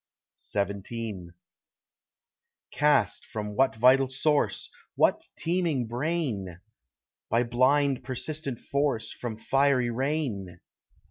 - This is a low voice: Yes, low, 125 Hz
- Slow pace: Yes, slow, 75 wpm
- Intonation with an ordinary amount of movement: Yes, average, 4.5 semitones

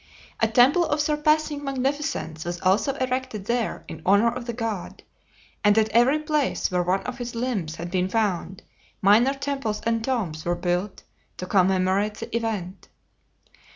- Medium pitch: No, high, 225 Hz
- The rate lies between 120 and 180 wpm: Yes, average, 155 wpm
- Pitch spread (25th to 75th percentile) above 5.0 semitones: Yes, wide, 5.6 semitones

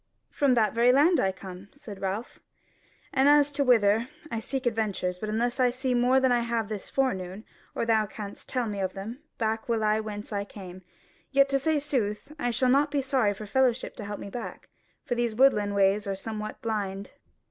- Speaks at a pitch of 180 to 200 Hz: No, high, 225 Hz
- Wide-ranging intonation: No, average, 4.1 semitones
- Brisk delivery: Yes, fast, 215 wpm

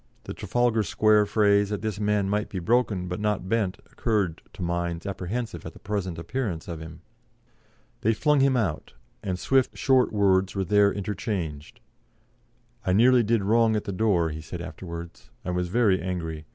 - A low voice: Yes, low, 100 Hz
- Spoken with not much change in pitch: No, average, 3.8 semitones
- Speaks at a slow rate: No, average, 175 wpm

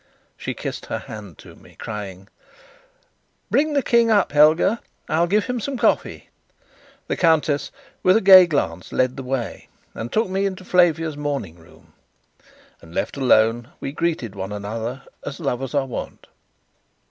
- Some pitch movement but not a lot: No, wide, 8.7 semitones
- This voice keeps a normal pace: Yes, average, 155 wpm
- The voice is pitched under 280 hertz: Yes, medium, 140 Hz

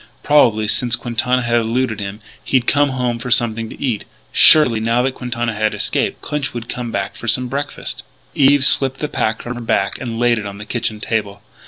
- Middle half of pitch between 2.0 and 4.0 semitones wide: Yes, narrow, 2.5 semitones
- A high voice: No, low, 120 Hz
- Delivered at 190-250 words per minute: Yes, fast, 205 wpm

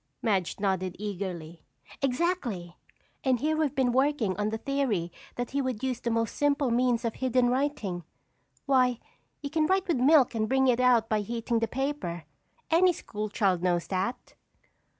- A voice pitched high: Yes, high, 240 Hz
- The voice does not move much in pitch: No, average, 5.1 semitones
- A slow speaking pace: No, average, 170 wpm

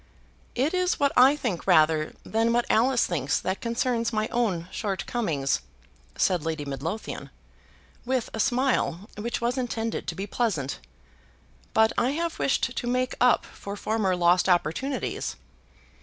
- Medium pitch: No, high, 225 Hz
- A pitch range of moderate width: No, wide, 5.8 semitones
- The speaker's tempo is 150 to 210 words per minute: No, average, 140 wpm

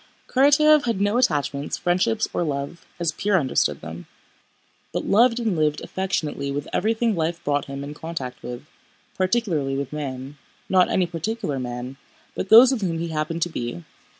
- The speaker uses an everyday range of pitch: No, wide, 6.3 semitones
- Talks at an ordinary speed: Yes, average, 160 wpm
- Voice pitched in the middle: Yes, medium, 165 Hz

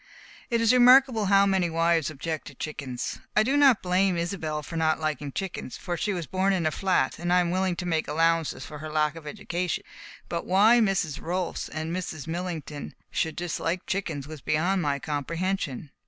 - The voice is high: No, medium, 170 Hz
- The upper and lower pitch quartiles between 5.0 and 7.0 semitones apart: No, average, 3.6 semitones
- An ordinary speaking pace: Yes, average, 190 wpm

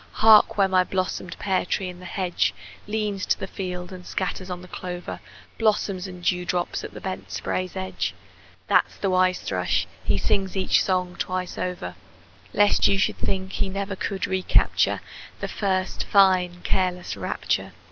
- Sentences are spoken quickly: No, average, 165 wpm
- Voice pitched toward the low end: No, medium, 185 Hz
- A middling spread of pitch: No, narrow, 1.2 semitones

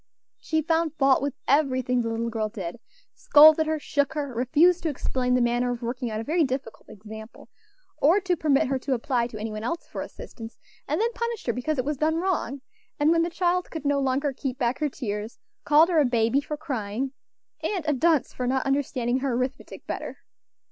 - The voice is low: No, very high, 270 Hz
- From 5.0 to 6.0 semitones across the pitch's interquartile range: No, average, 4.4 semitones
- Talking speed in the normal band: No, fast, 210 wpm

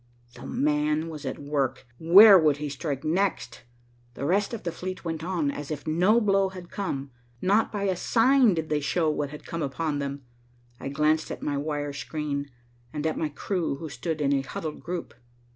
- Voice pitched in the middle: Yes, medium, 155 Hz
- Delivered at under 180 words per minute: No, average, 195 wpm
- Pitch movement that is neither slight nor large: Yes, average, 4.0 semitones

